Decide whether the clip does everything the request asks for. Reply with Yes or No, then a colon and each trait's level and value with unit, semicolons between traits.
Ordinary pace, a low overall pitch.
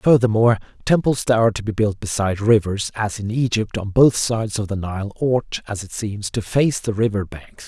No: fast, 210 wpm; low, 110 Hz